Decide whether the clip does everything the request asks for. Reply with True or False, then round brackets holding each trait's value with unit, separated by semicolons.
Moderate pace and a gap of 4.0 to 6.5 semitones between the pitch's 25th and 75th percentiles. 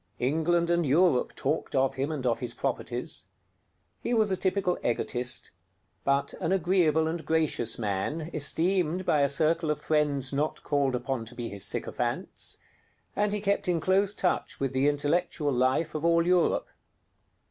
True (160 wpm; 4.4 semitones)